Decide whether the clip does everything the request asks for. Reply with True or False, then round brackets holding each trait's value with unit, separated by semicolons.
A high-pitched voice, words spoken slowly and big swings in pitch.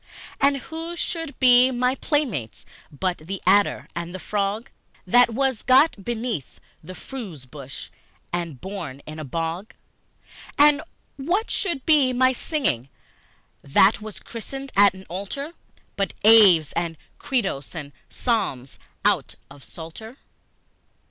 True (210 Hz; 130 wpm; 7.8 semitones)